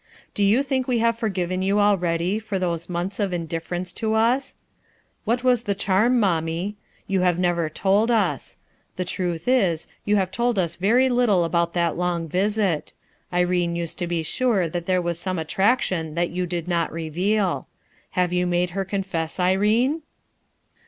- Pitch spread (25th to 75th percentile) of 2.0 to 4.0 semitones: Yes, average, 3.5 semitones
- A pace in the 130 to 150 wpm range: No, average, 170 wpm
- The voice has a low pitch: No, medium, 185 Hz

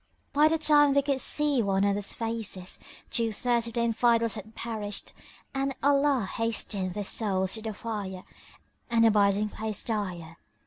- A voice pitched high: Yes, high, 225 Hz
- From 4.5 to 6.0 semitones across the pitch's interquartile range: No, average, 3.2 semitones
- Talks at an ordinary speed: Yes, average, 160 wpm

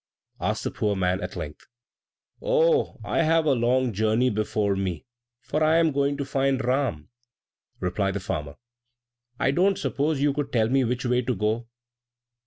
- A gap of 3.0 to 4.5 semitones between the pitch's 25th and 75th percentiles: No, average, 5.3 semitones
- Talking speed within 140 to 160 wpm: No, average, 170 wpm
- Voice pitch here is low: Yes, low, 125 Hz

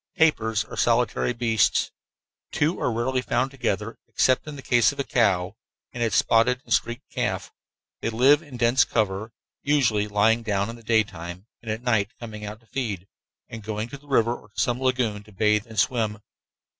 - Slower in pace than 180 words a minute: No, average, 190 wpm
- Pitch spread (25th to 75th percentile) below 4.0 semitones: Yes, average, 2.8 semitones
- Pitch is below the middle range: Yes, low, 115 Hz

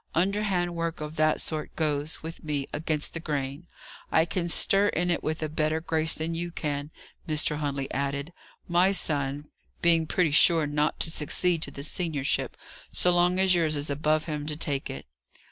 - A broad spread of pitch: No, narrow, 2.5 semitones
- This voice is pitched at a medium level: Yes, medium, 155 Hz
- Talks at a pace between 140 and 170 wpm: No, average, 180 wpm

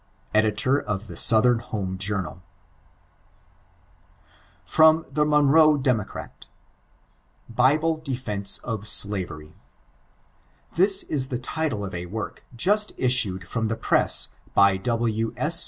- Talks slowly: Yes, slow, 110 wpm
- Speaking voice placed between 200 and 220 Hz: No, low, 115 Hz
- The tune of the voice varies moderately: No, wide, 6.4 semitones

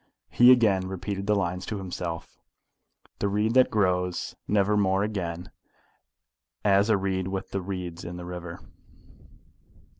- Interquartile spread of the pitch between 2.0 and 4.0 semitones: Yes, narrow, 2.4 semitones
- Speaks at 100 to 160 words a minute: Yes, average, 140 wpm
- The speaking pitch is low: Yes, very low, 95 Hz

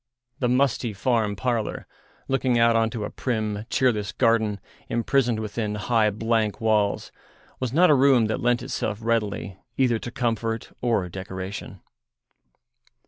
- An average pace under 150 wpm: Yes, average, 140 wpm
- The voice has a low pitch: Yes, low, 115 Hz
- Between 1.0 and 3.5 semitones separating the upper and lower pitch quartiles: Yes, narrow, 2.5 semitones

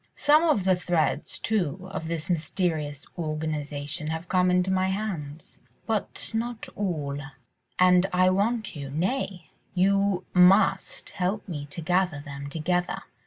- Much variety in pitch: No, average, 3.8 semitones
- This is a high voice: No, medium, 180 Hz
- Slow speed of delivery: Yes, slow, 130 wpm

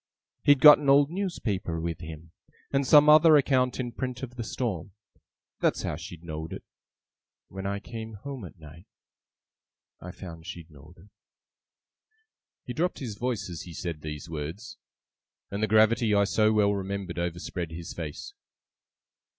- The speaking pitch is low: Yes, low, 100 Hz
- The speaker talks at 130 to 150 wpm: No, average, 160 wpm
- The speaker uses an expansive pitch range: Yes, wide, 7.0 semitones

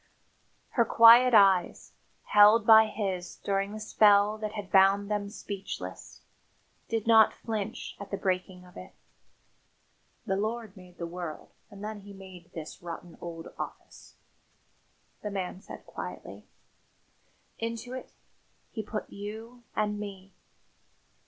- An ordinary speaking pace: No, slow, 130 wpm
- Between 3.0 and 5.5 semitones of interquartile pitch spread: No, narrow, 2.4 semitones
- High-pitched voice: Yes, high, 205 Hz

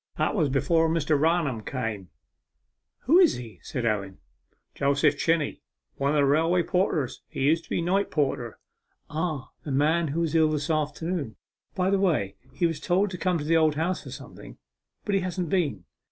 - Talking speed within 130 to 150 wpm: No, average, 185 wpm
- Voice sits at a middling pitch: Yes, medium, 155 Hz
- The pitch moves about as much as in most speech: Yes, average, 4.0 semitones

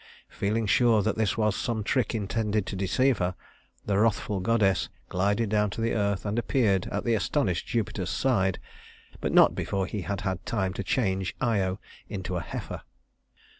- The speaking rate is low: No, average, 170 wpm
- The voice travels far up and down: No, average, 2.9 semitones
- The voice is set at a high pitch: No, low, 105 Hz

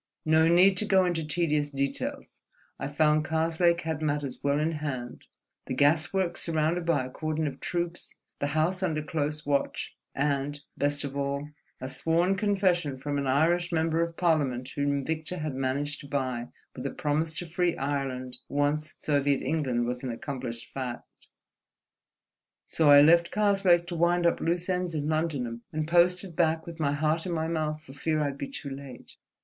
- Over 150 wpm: Yes, average, 175 wpm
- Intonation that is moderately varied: Yes, average, 3.1 semitones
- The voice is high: No, medium, 155 Hz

